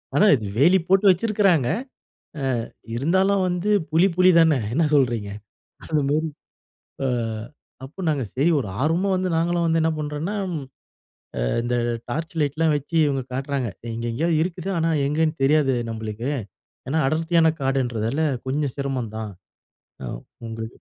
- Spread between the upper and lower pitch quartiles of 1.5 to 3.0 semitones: No, average, 4.2 semitones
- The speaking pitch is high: No, medium, 150 Hz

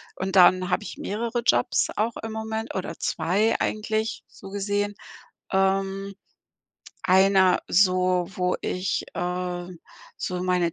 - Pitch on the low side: No, high, 195 Hz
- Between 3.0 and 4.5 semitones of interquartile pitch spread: No, narrow, 2.4 semitones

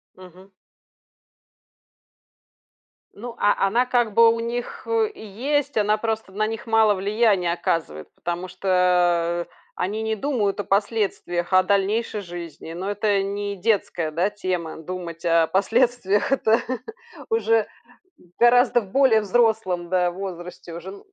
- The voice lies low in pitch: No, high, 200 Hz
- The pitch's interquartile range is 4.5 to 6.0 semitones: No, average, 3.9 semitones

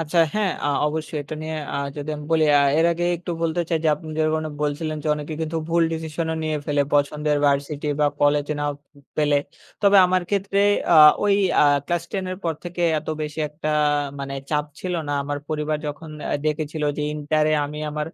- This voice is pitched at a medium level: Yes, medium, 155 Hz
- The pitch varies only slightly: Yes, narrow, 1.8 semitones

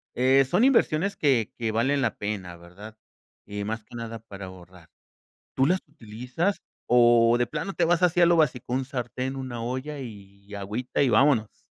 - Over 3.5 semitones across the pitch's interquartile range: Yes, average, 4.9 semitones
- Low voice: Yes, low, 120 Hz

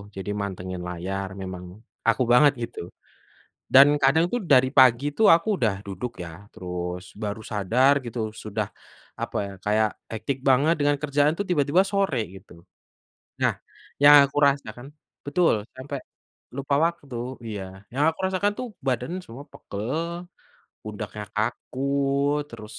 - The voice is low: Yes, low, 125 Hz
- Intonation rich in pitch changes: Yes, wide, 5.7 semitones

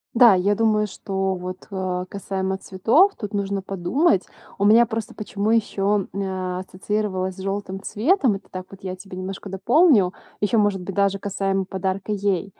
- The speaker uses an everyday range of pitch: No, narrow, 1.8 semitones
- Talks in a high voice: Yes, high, 195 Hz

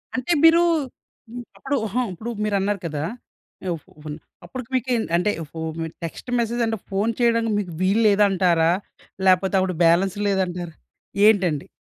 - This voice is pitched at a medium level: No, high, 195 Hz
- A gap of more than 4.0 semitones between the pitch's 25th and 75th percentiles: Yes, average, 4.4 semitones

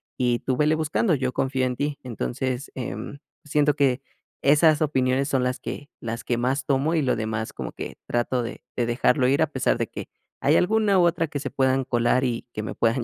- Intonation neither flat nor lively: Yes, average, 3.0 semitones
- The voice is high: No, low, 130 Hz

